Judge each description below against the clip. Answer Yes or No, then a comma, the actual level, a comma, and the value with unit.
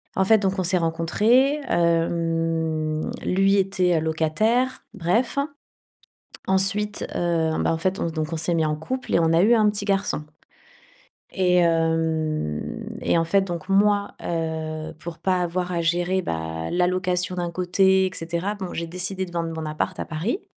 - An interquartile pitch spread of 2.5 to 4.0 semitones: Yes, average, 2.9 semitones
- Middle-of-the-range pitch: Yes, medium, 175 Hz